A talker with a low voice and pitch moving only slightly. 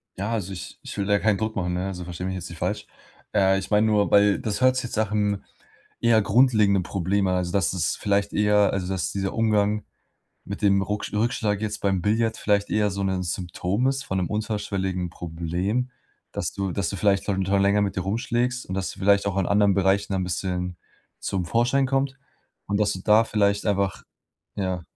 Yes: low, 100 Hz; narrow, 2.0 semitones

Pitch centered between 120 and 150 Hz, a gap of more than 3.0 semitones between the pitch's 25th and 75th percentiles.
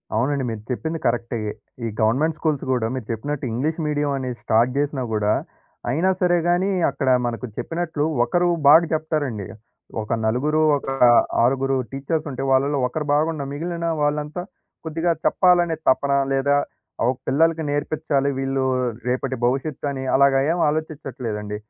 Yes: medium, 140 Hz; average, 3.4 semitones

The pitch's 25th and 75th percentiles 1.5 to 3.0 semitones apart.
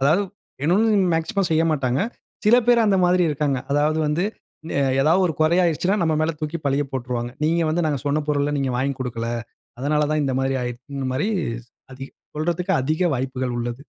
No: average, 3.9 semitones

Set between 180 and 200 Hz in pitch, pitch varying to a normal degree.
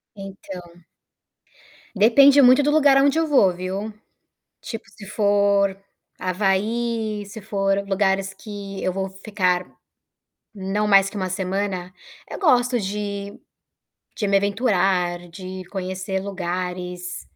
No: high, 195 Hz; narrow, 2.3 semitones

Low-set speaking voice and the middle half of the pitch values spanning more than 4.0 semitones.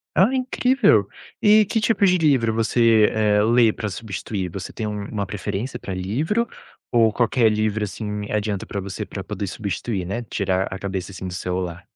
No: low, 105 Hz; average, 3.6 semitones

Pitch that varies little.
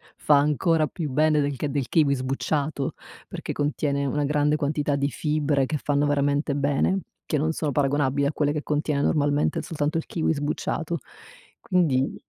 Yes: narrow, 1.4 semitones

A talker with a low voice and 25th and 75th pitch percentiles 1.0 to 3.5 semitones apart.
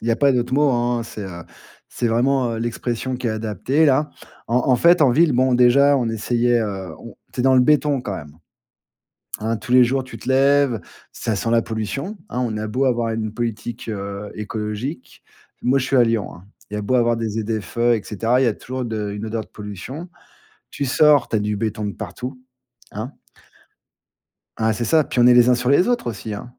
Yes: low, 120 Hz; average, 3.1 semitones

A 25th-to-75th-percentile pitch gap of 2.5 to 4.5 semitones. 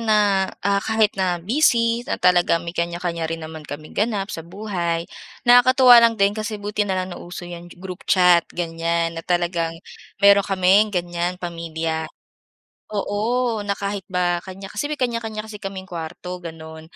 Yes: average, 3.6 semitones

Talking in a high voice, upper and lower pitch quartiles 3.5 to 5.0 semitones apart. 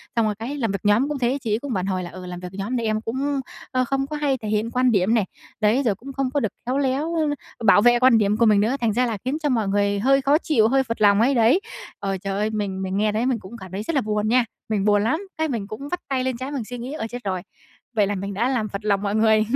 Yes: high, 225 Hz; average, 4.2 semitones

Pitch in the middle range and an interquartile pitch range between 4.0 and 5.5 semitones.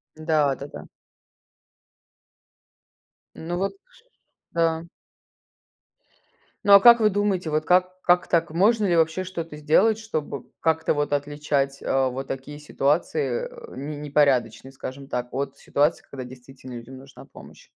Yes: medium, 150 Hz; average, 4.6 semitones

